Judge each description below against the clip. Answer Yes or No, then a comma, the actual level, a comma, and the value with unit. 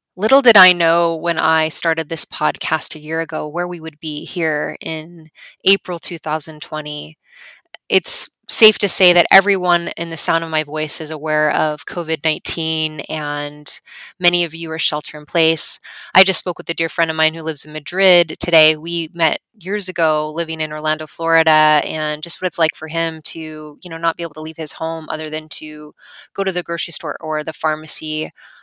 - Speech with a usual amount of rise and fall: No, narrow, 1.7 semitones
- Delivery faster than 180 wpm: Yes, average, 195 wpm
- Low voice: No, medium, 160 Hz